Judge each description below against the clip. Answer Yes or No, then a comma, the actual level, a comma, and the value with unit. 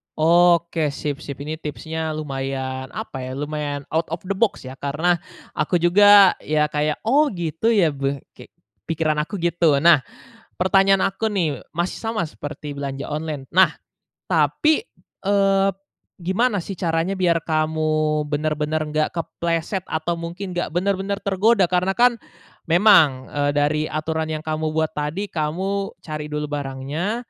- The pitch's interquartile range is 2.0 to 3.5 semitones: No, average, 3.9 semitones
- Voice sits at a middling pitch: Yes, medium, 160 Hz